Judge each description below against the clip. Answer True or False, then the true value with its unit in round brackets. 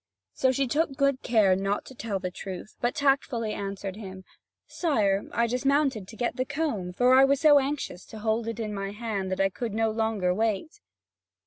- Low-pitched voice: False (225 Hz)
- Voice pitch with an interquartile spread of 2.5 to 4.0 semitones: False (5.0 semitones)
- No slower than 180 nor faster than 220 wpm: True (200 wpm)